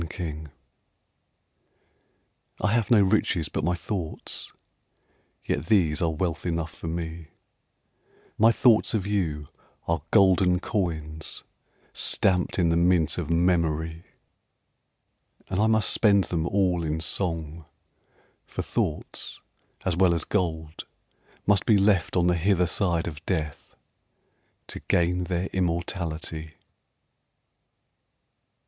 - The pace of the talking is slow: Yes, slow, 115 wpm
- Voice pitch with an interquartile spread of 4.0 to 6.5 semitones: No, average, 2.8 semitones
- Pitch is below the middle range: Yes, very low, 85 Hz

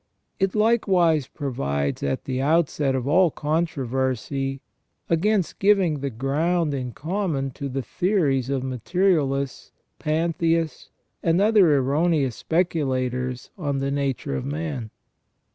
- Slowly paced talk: Yes, slow, 115 wpm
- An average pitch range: Yes, average, 4.3 semitones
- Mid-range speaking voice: Yes, medium, 145 Hz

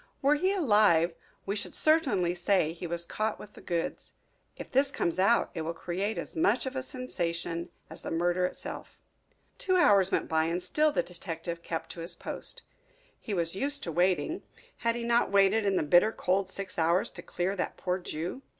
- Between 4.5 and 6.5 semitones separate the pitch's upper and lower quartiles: Yes, average, 5.3 semitones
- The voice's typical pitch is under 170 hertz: No, high, 190 Hz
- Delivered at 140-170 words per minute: No, average, 195 wpm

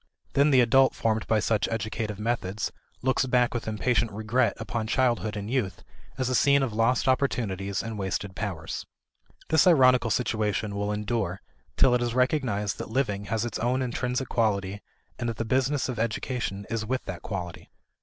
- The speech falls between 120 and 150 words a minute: No, average, 175 wpm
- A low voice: Yes, low, 115 Hz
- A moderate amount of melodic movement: Yes, average, 3.5 semitones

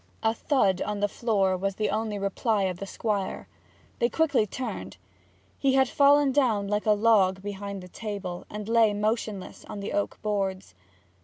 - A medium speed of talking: Yes, average, 170 wpm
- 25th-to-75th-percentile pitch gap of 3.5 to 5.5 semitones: No, narrow, 2.5 semitones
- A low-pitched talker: No, high, 210 Hz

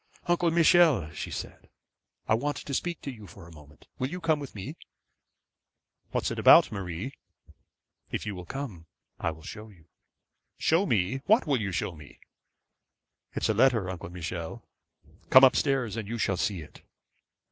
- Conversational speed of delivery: Yes, average, 175 wpm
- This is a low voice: Yes, low, 110 Hz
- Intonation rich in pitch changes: Yes, wide, 8.0 semitones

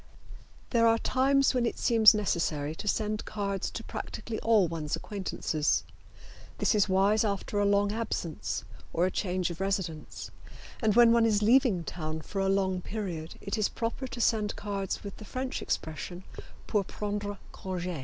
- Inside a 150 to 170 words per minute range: Yes, average, 165 wpm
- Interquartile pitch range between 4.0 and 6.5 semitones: No, average, 3.4 semitones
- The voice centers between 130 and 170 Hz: No, high, 205 Hz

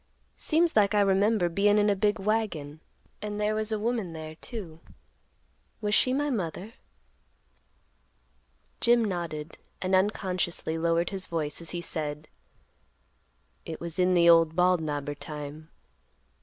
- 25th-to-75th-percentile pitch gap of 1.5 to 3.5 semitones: No, average, 4.6 semitones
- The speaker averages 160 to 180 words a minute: No, average, 140 wpm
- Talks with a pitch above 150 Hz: Yes, medium, 185 Hz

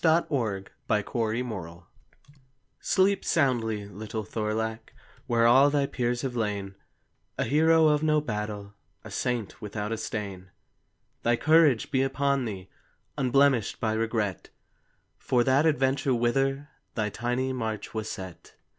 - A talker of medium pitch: No, low, 120 Hz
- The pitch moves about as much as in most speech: Yes, average, 4.3 semitones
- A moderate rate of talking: No, slow, 130 wpm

